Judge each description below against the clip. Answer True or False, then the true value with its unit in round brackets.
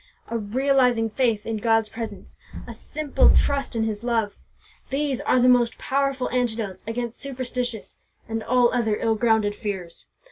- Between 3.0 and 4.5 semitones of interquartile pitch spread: False (2.4 semitones)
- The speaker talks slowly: False (150 wpm)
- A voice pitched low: False (235 Hz)